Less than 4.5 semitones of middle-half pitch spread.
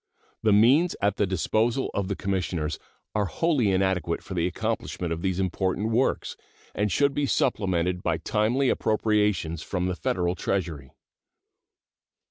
Yes: average, 3.6 semitones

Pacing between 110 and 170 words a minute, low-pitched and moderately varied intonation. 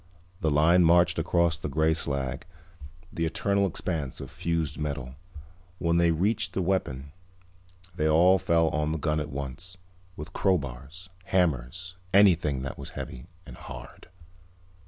Yes: average, 140 wpm; very low, 80 Hz; average, 3.6 semitones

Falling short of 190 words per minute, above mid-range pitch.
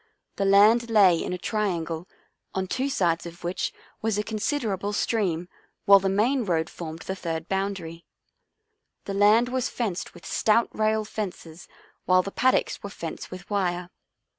Yes: average, 160 wpm; high, 195 Hz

